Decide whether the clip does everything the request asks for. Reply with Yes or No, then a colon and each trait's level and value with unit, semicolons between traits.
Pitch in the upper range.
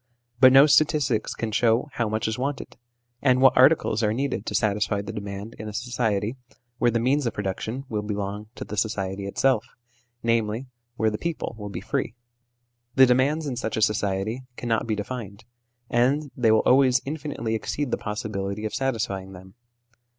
No: low, 110 Hz